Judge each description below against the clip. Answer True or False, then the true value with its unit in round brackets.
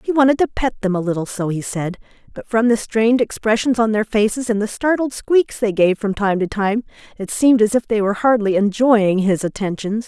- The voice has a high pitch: True (215 Hz)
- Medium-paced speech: False (225 wpm)